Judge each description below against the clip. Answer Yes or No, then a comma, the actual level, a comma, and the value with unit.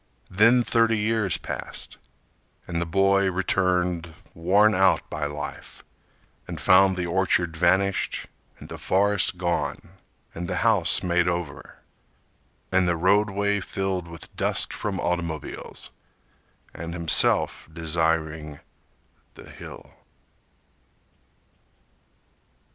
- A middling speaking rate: No, slow, 105 wpm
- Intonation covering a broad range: No, average, 2.7 semitones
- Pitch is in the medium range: No, very low, 90 Hz